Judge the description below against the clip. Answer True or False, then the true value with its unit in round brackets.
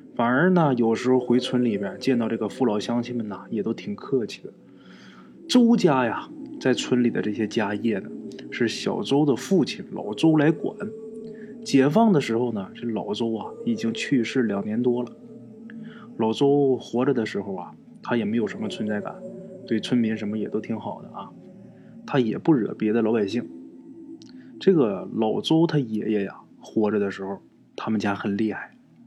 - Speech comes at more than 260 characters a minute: False (250 characters per minute)